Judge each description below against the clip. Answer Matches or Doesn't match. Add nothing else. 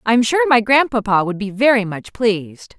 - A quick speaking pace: Doesn't match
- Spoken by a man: Doesn't match